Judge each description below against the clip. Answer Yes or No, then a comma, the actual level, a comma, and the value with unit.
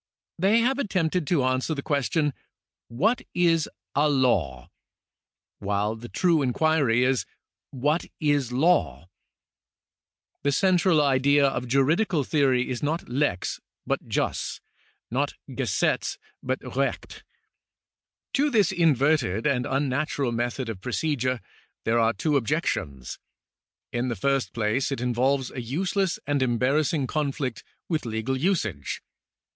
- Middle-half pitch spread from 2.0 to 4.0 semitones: No, average, 4.4 semitones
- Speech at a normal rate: No, slow, 130 wpm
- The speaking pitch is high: No, low, 135 Hz